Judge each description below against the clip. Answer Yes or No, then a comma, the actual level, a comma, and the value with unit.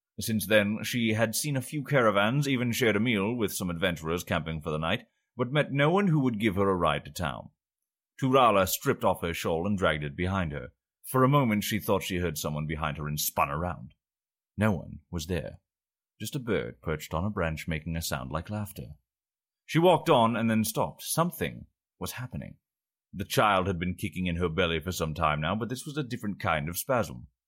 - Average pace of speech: No, fast, 215 wpm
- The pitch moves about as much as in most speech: No, wide, 6.2 semitones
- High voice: No, very low, 95 Hz